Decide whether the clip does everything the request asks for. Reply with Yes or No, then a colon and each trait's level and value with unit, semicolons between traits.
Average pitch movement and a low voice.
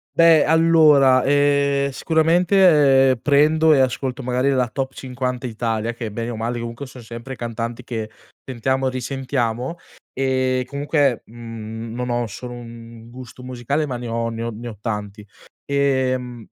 Yes: average, 3.1 semitones; low, 125 Hz